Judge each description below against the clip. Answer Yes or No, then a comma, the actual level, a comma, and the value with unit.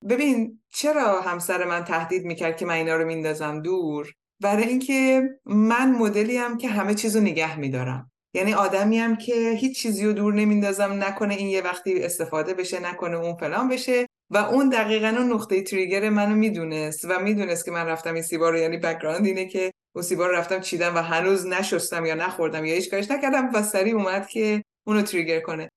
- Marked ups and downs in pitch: No, average, 4.4 semitones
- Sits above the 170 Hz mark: Yes, high, 190 Hz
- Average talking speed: No, fast, 190 wpm